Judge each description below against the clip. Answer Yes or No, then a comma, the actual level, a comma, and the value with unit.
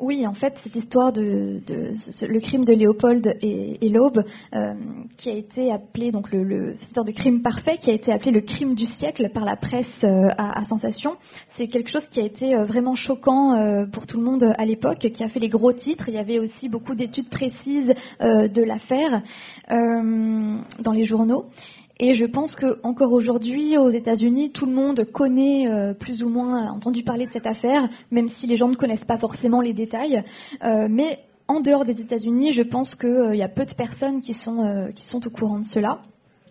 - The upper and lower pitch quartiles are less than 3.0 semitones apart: Yes, narrow, 2.5 semitones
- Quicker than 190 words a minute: Yes, average, 215 wpm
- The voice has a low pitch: No, high, 235 Hz